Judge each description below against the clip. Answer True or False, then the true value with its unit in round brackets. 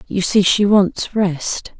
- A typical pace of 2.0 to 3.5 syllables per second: True (3.2 syllables/s)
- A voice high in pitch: True (195 Hz)